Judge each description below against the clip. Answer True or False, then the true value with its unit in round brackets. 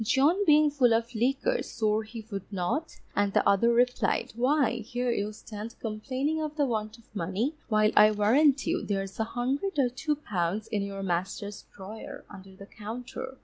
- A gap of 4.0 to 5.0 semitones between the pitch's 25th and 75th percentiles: True (4.7 semitones)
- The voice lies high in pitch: True (225 Hz)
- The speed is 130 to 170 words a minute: False (180 wpm)